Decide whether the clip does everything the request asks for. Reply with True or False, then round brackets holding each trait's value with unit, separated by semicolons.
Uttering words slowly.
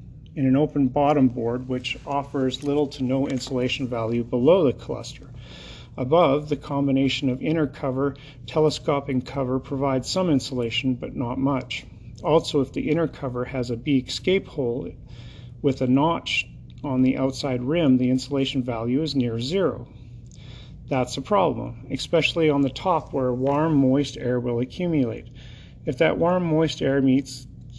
False (155 wpm)